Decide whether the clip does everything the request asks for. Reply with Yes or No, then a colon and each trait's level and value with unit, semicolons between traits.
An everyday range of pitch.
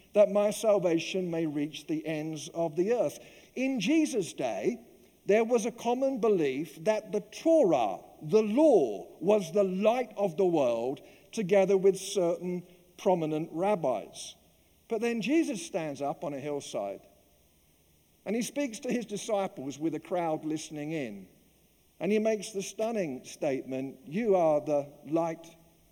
No: wide, 5.8 semitones